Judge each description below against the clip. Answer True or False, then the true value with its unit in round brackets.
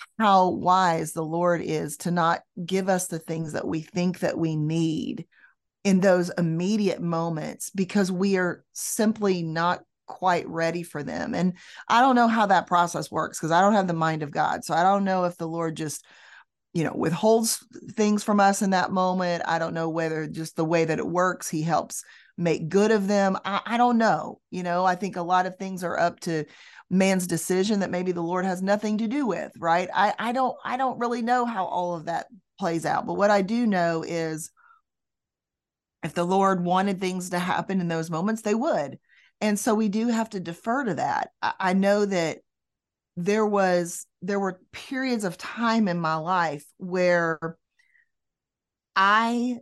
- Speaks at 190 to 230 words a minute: True (195 wpm)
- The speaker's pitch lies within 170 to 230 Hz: True (185 Hz)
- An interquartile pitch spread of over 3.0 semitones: True (3.7 semitones)